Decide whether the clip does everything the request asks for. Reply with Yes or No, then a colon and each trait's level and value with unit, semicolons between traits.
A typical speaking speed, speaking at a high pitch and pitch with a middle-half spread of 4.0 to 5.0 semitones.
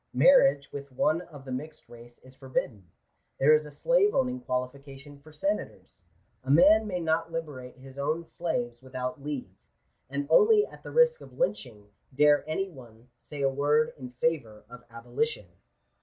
No: average, 165 wpm; medium, 140 Hz; average, 4.5 semitones